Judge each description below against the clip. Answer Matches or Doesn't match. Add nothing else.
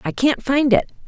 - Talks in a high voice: Matches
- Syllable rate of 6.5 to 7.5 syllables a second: Doesn't match